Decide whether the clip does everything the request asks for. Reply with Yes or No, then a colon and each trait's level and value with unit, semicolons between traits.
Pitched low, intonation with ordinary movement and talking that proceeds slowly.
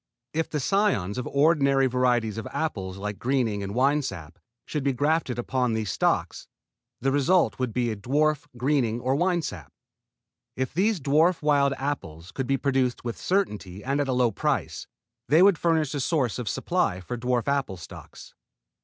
No: low, 130 Hz; average, 4.5 semitones; average, 170 wpm